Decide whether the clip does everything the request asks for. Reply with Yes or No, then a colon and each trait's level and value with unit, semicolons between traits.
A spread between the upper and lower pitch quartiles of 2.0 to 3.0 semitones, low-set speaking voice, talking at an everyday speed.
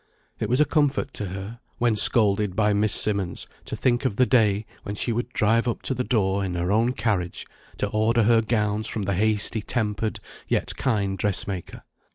Yes: average, 2.7 semitones; low, 110 Hz; average, 195 wpm